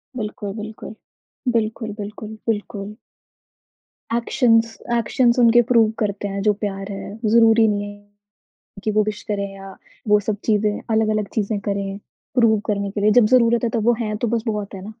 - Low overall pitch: No, high, 215 Hz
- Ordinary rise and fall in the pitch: No, narrow, 1.8 semitones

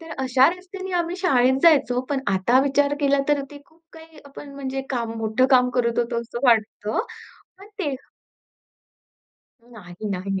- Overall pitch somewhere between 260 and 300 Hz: Yes, very high, 265 Hz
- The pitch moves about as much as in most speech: Yes, average, 3.9 semitones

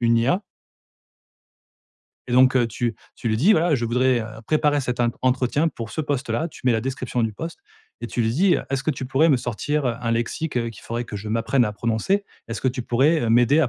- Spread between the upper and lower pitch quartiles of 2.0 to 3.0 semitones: No, average, 3.7 semitones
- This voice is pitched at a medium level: No, low, 125 Hz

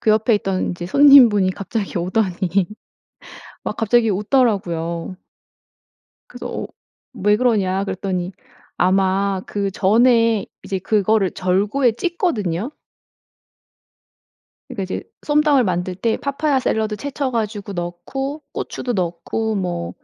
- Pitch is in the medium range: No, high, 205 Hz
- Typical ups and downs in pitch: Yes, average, 4.3 semitones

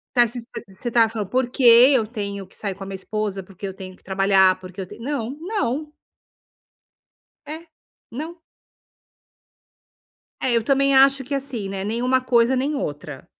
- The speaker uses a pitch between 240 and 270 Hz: No, high, 230 Hz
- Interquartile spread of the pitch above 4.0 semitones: Yes, wide, 5.4 semitones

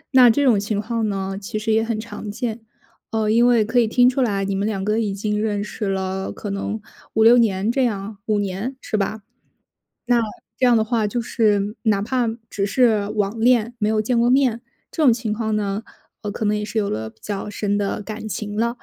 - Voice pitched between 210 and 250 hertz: Yes, high, 215 Hz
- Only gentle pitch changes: Yes, narrow, 2.3 semitones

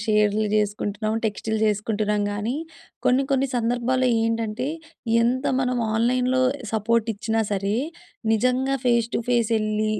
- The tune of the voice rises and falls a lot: No, average, 2.8 semitones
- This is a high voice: Yes, high, 225 Hz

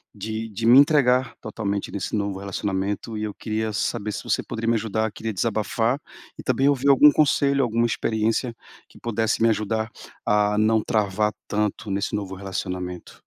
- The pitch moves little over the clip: Yes, narrow, 2.3 semitones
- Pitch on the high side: No, low, 110 Hz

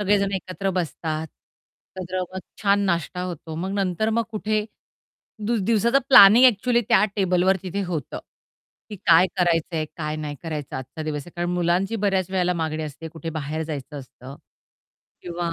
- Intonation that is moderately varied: Yes, average, 3.7 semitones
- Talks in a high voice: No, medium, 180 Hz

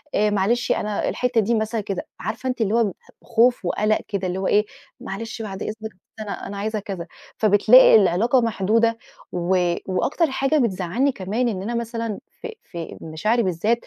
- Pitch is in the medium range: No, high, 215 Hz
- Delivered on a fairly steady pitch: No, average, 3.3 semitones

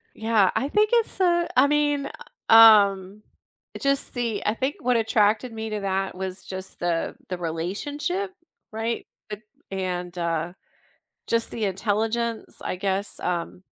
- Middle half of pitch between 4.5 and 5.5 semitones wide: Yes, average, 4.9 semitones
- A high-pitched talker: Yes, high, 215 Hz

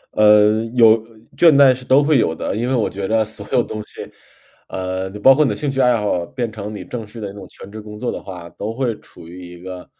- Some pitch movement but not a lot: Yes, average, 3.6 semitones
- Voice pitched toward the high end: No, low, 110 Hz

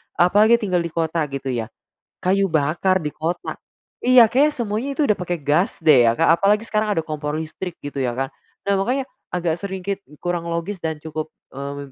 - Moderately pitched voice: Yes, medium, 175 Hz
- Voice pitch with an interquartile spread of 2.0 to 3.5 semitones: No, average, 4.7 semitones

